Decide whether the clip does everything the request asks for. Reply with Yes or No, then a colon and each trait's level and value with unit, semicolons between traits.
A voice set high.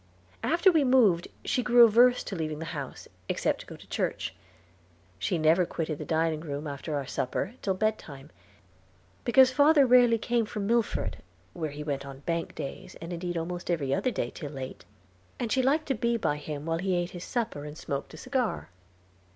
No: medium, 175 Hz